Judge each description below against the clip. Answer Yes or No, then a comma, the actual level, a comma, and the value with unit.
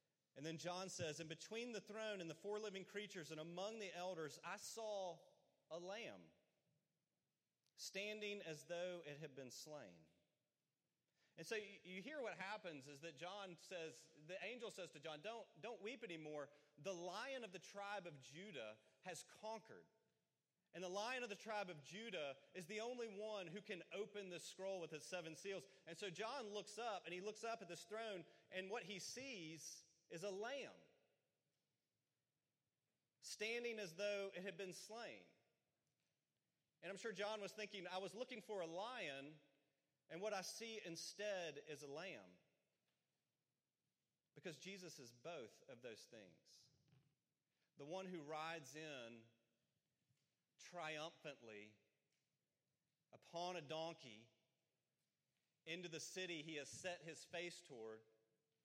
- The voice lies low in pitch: No, medium, 175 Hz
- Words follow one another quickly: No, average, 150 wpm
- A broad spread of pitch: No, average, 5.0 semitones